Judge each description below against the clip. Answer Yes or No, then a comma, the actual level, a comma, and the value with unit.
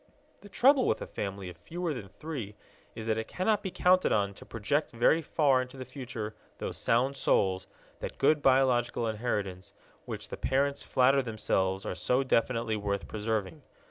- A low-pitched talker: Yes, low, 120 Hz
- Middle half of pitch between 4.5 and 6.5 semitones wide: Yes, average, 5.1 semitones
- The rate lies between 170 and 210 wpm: Yes, average, 175 wpm